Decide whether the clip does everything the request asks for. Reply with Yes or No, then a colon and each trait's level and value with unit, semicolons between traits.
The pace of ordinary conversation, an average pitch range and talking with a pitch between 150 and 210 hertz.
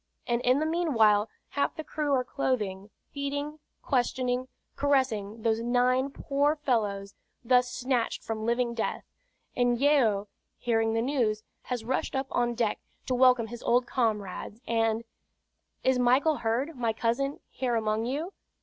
No: average, 145 wpm; average, 3.1 semitones; high, 245 Hz